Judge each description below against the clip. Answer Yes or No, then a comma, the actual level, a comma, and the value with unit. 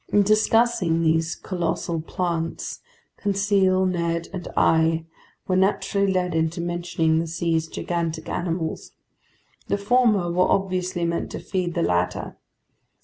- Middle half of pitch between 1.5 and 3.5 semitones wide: Yes, narrow, 2.5 semitones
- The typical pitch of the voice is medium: Yes, medium, 175 Hz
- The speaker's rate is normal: No, slow, 125 wpm